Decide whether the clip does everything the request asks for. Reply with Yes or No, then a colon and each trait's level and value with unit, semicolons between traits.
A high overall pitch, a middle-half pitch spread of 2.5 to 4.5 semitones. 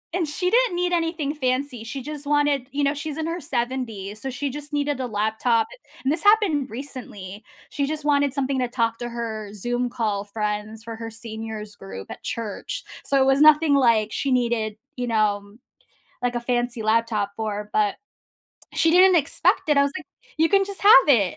No: very high, 250 Hz; average, 4.9 semitones